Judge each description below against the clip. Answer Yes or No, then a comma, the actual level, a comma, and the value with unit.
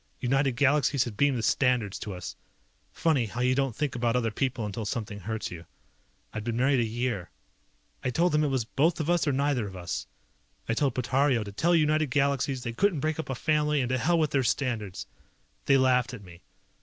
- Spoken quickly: Yes, fast, 215 wpm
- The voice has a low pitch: Yes, low, 130 Hz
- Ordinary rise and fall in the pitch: Yes, average, 3.9 semitones